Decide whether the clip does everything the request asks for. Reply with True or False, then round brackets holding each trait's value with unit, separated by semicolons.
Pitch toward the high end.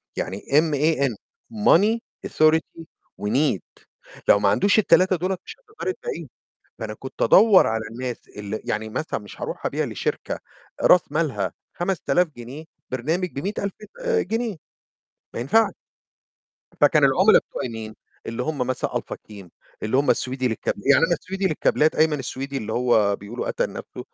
False (140 Hz)